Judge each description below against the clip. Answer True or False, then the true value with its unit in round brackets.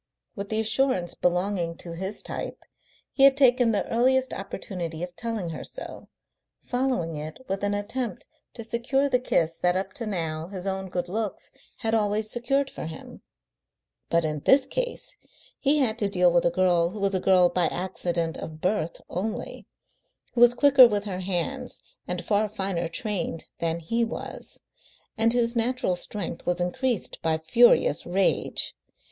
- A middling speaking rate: True (165 wpm)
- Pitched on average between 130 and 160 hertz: False (195 Hz)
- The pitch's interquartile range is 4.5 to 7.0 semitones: True (5.2 semitones)